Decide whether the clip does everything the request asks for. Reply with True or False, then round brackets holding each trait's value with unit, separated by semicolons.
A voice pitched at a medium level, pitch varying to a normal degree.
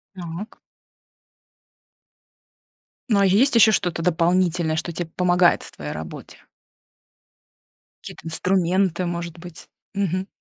False (175 Hz; 2.1 semitones)